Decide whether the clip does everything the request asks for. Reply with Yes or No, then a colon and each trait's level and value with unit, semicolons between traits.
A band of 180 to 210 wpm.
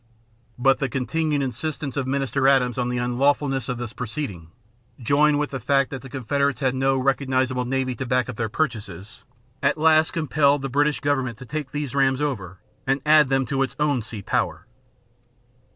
Yes: average, 185 wpm